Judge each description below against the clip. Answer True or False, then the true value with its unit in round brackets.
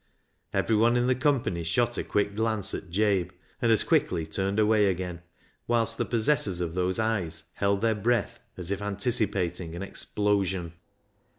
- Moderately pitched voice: False (100 Hz)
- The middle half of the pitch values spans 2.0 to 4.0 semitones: True (3.6 semitones)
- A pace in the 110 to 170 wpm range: True (160 wpm)